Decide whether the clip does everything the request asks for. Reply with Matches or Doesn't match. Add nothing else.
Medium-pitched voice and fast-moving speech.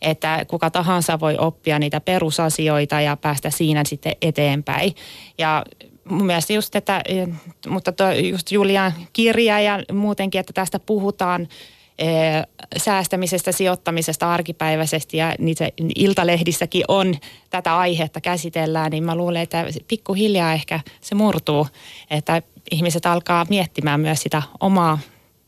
Doesn't match